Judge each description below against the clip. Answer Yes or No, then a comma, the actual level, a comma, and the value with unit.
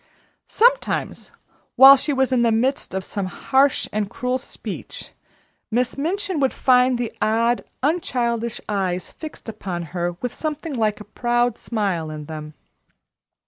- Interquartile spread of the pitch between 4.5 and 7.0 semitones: Yes, average, 4.9 semitones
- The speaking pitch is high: Yes, high, 240 Hz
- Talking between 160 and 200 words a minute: No, average, 145 wpm